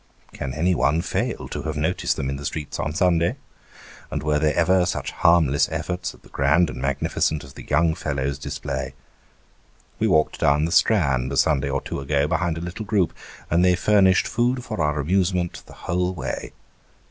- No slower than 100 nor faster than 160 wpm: No, average, 185 wpm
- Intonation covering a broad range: No, average, 3.9 semitones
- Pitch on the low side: Yes, very low, 80 Hz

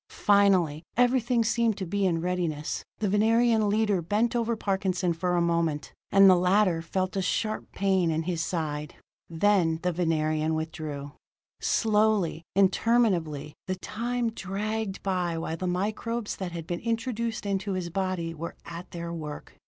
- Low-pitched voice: No, medium, 185 Hz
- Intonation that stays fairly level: No, average, 4.2 semitones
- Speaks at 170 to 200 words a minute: No, average, 150 wpm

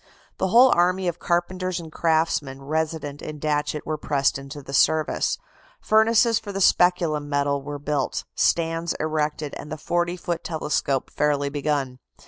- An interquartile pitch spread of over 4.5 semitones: No, average, 3.1 semitones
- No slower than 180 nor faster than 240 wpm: No, average, 150 wpm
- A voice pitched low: No, medium, 155 Hz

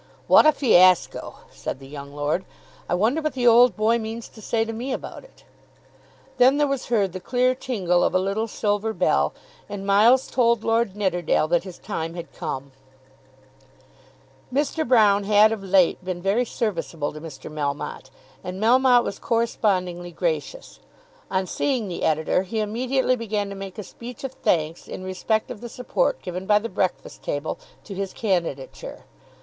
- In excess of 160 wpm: Yes, average, 170 wpm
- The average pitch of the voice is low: No, high, 205 Hz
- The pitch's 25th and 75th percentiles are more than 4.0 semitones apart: Yes, average, 5.0 semitones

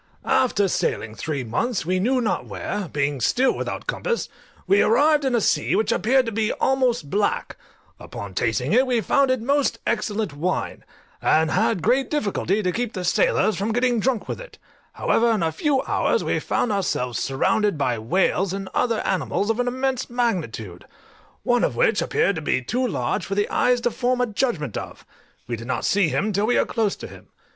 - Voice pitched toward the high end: Yes, high, 215 Hz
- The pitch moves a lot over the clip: Yes, wide, 6.7 semitones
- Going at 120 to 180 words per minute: No, average, 195 wpm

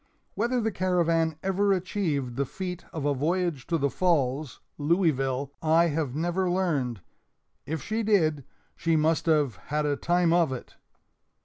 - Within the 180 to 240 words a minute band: No, average, 150 wpm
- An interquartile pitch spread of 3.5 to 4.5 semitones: Yes, average, 4.0 semitones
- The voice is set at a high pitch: No, medium, 165 Hz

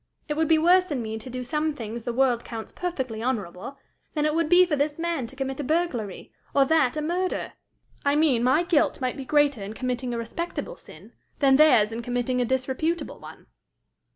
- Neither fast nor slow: No, fast, 210 wpm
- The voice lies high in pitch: Yes, very high, 270 Hz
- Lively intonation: No, average, 4.4 semitones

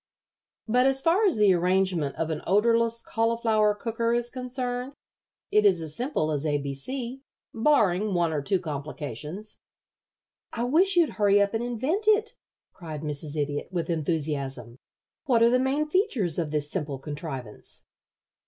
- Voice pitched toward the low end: No, high, 205 Hz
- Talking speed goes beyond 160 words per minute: No, average, 155 wpm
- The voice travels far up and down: Yes, wide, 8.1 semitones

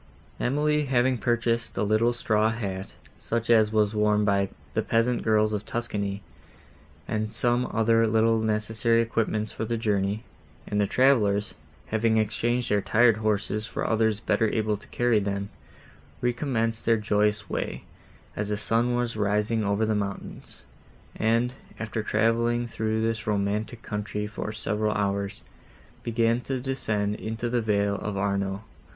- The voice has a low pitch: Yes, low, 110 Hz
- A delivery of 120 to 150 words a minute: Yes, average, 145 wpm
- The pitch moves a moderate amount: No, narrow, 1.8 semitones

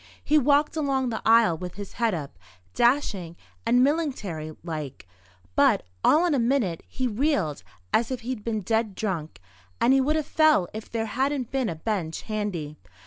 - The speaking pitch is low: No, high, 225 Hz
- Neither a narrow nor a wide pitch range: No, wide, 7.0 semitones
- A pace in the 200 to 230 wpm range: No, average, 175 wpm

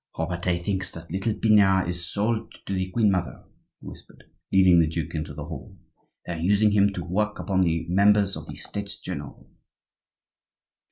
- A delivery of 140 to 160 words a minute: No, average, 175 wpm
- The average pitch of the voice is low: Yes, very low, 95 Hz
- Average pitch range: Yes, average, 3.0 semitones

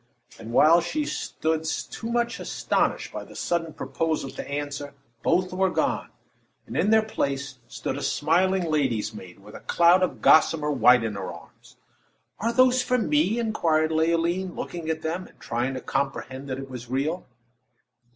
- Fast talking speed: No, average, 175 wpm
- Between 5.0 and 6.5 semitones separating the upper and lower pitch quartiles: Yes, wide, 5.4 semitones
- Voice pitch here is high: No, medium, 160 Hz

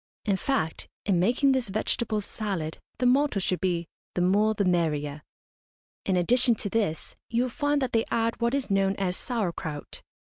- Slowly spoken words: No, average, 180 wpm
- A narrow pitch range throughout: No, average, 5.0 semitones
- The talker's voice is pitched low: No, high, 205 Hz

